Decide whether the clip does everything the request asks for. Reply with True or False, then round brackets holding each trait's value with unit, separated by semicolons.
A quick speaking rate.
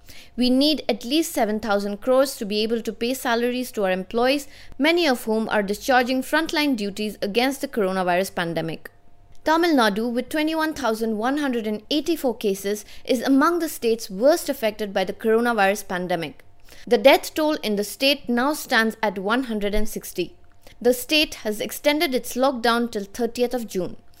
False (150 wpm)